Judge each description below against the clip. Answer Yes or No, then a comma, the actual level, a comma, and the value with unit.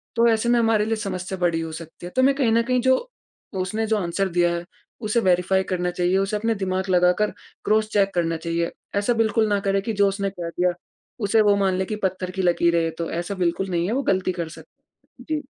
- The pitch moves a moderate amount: Yes, average, 3.6 semitones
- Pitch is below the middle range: No, high, 190 Hz